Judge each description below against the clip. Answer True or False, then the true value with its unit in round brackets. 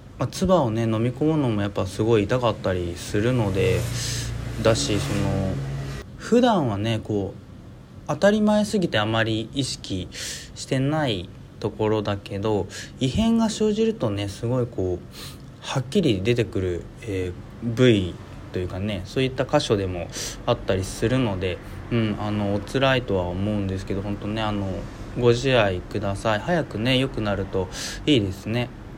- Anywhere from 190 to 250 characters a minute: False (300 characters per minute)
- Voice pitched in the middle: False (110 Hz)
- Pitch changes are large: False (4.2 semitones)